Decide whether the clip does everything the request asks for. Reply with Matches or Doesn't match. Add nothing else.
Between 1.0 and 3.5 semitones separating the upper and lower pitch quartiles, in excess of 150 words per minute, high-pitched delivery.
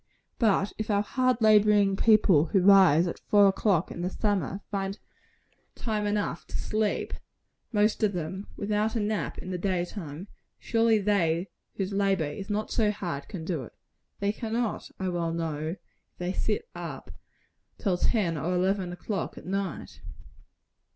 Matches